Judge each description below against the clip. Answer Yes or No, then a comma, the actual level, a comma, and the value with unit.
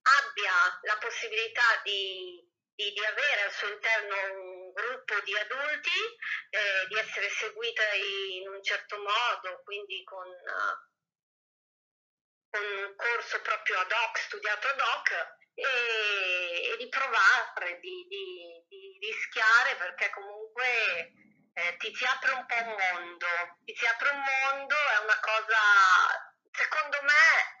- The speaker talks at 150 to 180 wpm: No, average, 135 wpm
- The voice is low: No, high, 230 Hz